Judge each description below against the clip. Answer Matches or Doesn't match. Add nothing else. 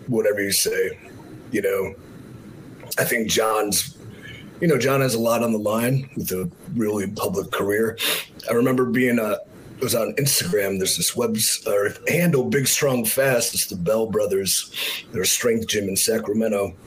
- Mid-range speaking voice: Doesn't match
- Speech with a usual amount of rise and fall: Matches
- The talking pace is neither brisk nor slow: Matches